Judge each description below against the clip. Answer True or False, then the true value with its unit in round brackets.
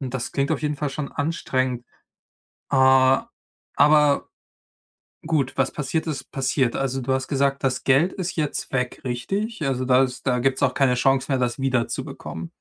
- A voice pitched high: False (135 Hz)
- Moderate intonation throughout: False (1.8 semitones)